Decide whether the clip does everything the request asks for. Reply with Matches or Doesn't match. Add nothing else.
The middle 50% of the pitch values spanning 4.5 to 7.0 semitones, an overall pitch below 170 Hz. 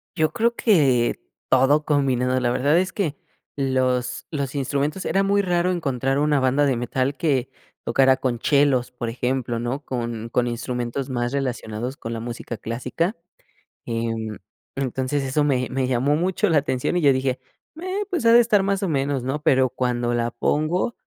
Doesn't match